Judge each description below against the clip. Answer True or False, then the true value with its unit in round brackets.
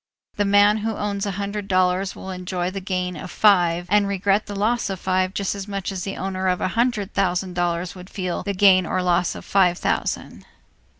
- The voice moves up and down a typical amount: False (1.8 semitones)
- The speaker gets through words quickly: True (215 wpm)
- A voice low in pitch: False (190 Hz)